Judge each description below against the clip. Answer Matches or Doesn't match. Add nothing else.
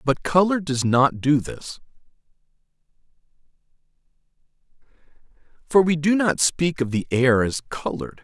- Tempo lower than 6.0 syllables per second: Matches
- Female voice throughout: Doesn't match